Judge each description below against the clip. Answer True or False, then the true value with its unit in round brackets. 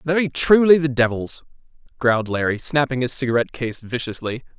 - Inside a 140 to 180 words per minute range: True (145 wpm)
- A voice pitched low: True (130 Hz)